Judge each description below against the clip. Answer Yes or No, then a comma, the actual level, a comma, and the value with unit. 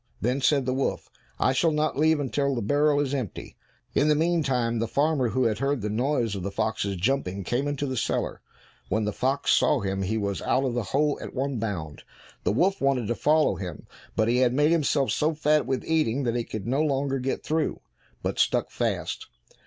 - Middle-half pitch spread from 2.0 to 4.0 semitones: No, average, 4.5 semitones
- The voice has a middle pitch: No, low, 130 Hz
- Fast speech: Yes, fast, 215 wpm